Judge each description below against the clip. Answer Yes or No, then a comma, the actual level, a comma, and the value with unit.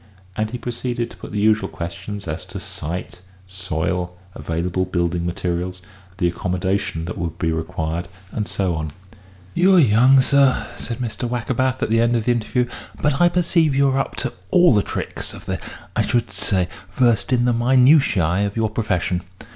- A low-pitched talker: Yes, low, 105 Hz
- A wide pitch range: Yes, wide, 5.8 semitones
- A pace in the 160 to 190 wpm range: Yes, average, 180 wpm